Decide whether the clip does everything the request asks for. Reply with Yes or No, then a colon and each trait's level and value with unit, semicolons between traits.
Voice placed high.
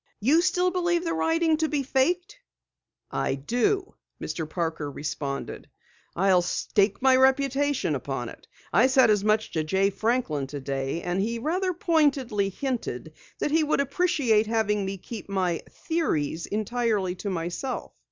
Yes: high, 225 Hz